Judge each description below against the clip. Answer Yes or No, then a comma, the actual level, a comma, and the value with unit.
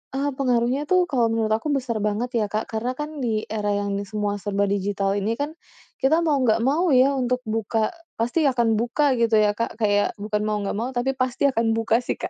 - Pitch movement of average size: Yes, average, 3.3 semitones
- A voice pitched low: No, high, 230 Hz